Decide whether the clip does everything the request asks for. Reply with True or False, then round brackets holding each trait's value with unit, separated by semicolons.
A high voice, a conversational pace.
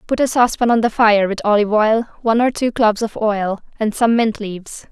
False (220 Hz; 230 wpm)